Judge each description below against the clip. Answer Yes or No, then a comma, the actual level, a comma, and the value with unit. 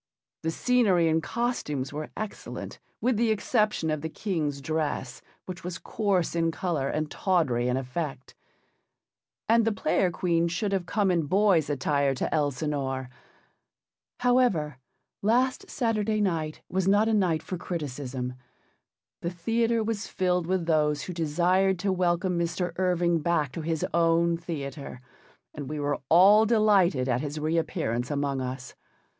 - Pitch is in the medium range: Yes, medium, 170 Hz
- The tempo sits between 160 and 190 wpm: No, average, 150 wpm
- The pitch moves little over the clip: No, average, 4.7 semitones